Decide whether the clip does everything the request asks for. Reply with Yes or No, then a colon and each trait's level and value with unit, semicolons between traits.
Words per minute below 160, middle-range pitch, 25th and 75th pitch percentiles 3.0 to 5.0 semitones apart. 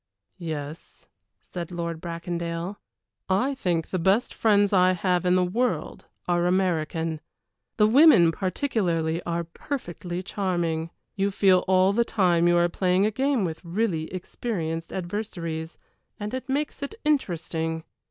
Yes: slow, 135 wpm; medium, 180 Hz; average, 3.4 semitones